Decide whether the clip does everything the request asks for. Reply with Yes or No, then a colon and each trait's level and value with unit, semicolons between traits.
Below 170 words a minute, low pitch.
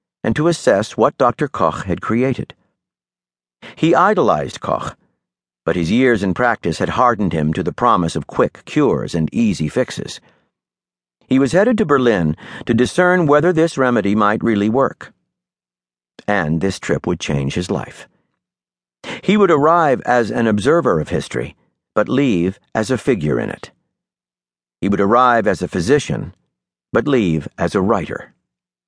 Yes: average, 155 wpm; very low, 95 Hz